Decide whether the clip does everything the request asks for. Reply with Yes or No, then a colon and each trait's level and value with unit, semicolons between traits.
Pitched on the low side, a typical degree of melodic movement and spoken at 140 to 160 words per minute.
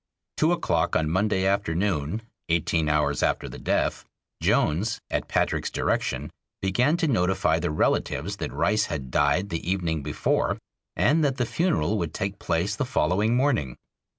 No: very low, 95 Hz; wide, 5.8 semitones; average, 150 wpm